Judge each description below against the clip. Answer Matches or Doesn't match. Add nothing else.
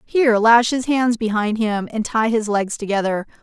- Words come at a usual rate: Matches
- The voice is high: Matches